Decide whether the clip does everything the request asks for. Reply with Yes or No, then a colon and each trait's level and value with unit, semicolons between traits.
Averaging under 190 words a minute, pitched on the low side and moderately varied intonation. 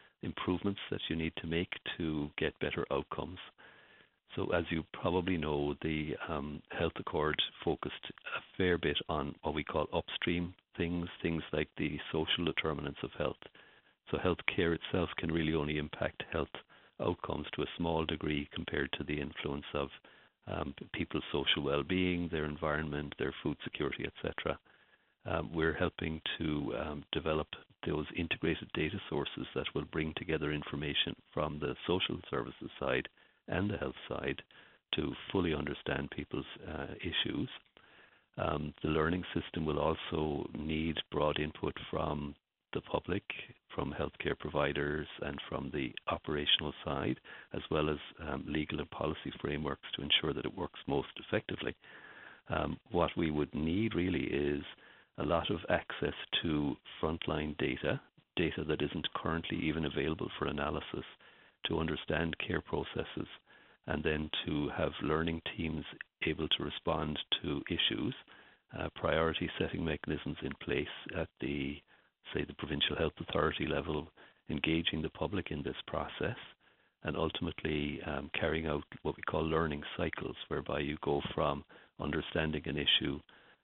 No: average, 145 wpm; very low, 80 Hz; narrow, 1.9 semitones